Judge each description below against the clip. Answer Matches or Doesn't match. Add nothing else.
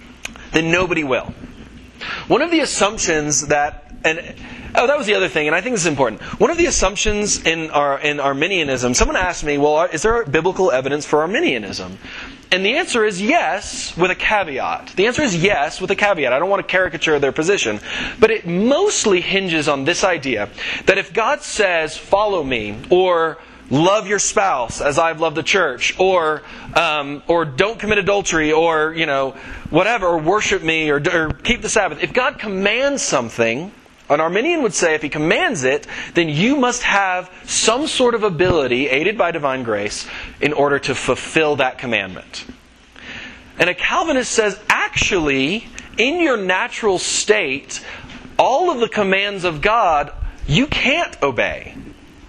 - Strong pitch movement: Matches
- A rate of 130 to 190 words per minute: Matches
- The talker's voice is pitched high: Doesn't match